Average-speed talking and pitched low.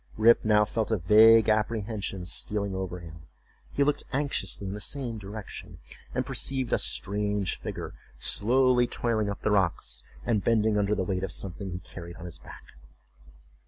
Yes: average, 165 wpm; low, 105 Hz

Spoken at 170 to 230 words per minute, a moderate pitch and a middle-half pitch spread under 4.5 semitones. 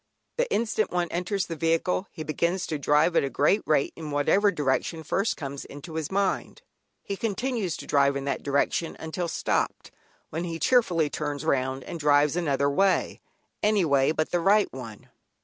No: average, 180 wpm; medium, 160 Hz; average, 4.8 semitones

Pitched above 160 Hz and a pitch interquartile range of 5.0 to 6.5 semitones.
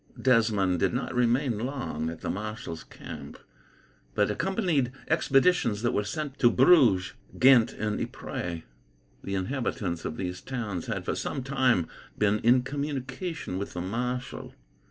No: low, 120 Hz; wide, 5.4 semitones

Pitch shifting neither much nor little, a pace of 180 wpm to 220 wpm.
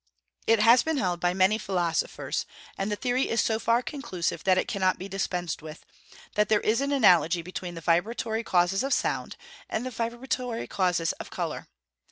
Yes: average, 4.7 semitones; average, 185 wpm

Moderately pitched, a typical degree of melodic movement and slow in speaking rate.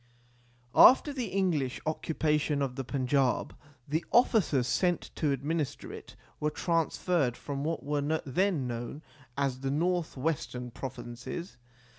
Yes: medium, 150 Hz; average, 4.0 semitones; slow, 125 wpm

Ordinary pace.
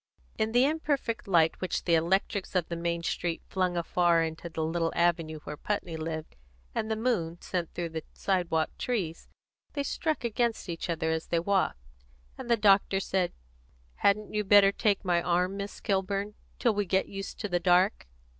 Yes: average, 180 wpm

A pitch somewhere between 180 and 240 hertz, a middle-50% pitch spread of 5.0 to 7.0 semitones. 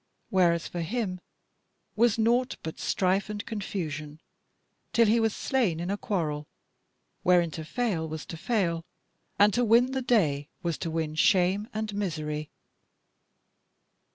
Yes: medium, 185 Hz; wide, 5.4 semitones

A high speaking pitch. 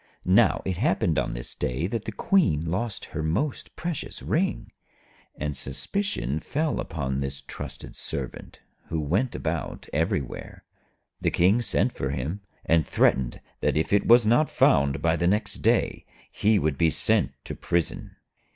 No: very low, 85 Hz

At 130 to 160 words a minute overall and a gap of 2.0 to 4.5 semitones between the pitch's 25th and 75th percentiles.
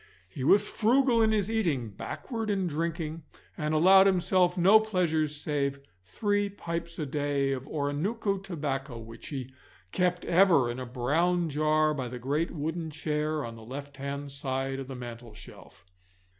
No: average, 155 wpm; average, 5.0 semitones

